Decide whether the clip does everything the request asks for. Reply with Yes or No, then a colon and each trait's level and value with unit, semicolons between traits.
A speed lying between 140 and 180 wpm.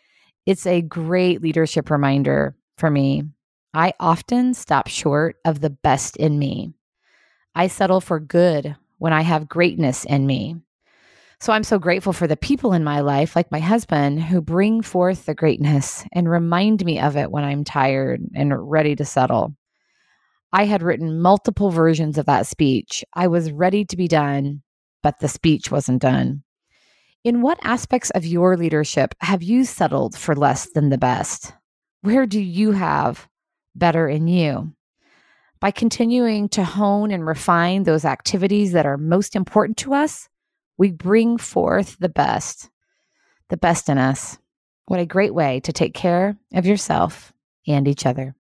Yes: average, 160 wpm